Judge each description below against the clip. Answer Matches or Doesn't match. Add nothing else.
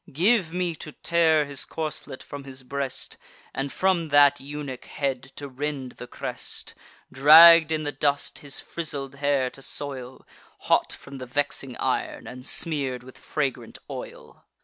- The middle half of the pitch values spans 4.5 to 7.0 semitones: Doesn't match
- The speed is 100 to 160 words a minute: Matches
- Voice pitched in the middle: Matches